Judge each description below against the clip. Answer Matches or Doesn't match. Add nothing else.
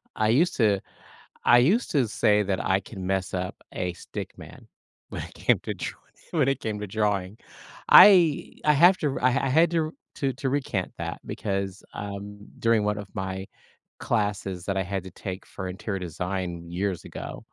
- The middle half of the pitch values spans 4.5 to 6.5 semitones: Matches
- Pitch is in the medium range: Doesn't match